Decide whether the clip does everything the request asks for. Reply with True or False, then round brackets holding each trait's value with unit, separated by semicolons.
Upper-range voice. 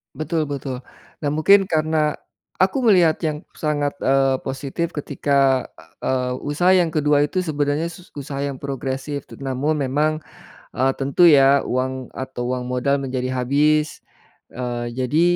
False (140 Hz)